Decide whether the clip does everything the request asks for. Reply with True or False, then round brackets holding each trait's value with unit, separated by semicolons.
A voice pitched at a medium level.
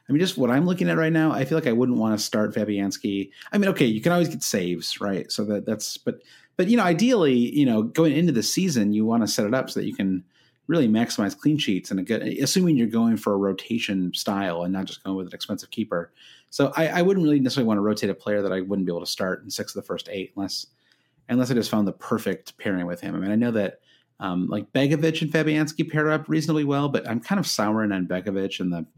False (115 Hz)